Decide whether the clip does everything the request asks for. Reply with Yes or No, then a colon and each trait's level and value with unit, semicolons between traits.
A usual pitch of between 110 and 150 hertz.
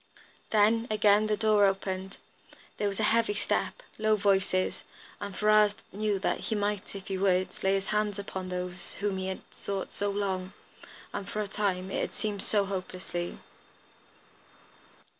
No: high, 200 Hz